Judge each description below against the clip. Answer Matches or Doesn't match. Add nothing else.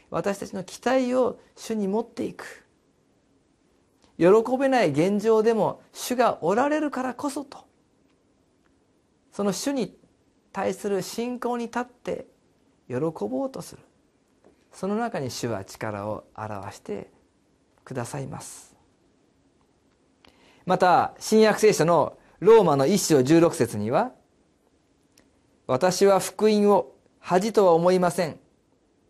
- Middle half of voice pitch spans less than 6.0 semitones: Matches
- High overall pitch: Matches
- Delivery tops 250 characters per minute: Doesn't match